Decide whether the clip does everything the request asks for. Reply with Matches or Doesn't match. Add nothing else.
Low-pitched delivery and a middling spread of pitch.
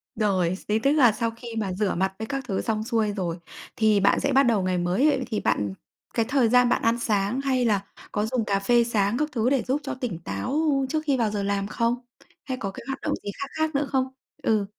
Doesn't match